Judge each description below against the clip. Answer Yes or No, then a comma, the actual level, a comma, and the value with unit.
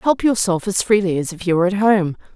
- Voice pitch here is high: Yes, high, 195 Hz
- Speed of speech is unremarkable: No, fast, 255 wpm